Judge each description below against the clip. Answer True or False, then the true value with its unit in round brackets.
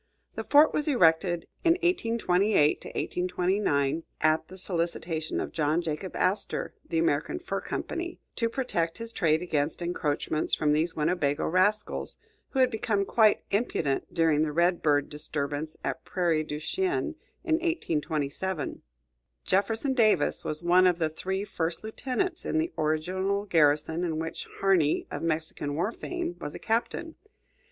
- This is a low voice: False (175 Hz)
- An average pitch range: False (5.9 semitones)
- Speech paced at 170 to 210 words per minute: False (145 wpm)